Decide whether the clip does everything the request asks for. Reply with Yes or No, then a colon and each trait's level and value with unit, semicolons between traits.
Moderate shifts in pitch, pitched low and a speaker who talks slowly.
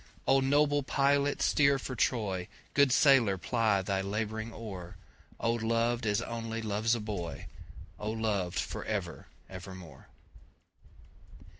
Yes: average, 4.5 semitones; low, 115 Hz; slow, 110 wpm